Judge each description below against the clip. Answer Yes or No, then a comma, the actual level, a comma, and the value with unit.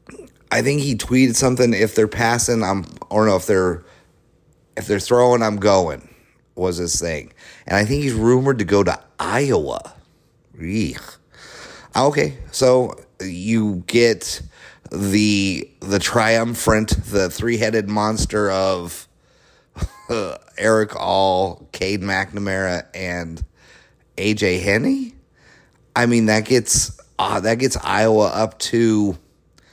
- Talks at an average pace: No, slow, 120 wpm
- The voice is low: Yes, low, 105 Hz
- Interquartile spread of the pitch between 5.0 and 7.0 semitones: No, average, 3.7 semitones